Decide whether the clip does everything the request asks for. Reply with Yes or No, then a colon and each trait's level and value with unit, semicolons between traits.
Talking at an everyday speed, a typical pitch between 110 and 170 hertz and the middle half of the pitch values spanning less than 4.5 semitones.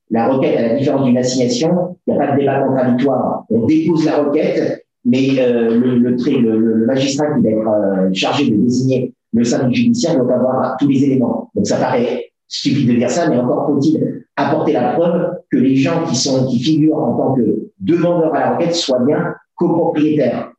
Yes: average, 205 wpm; low, 135 Hz; average, 4.1 semitones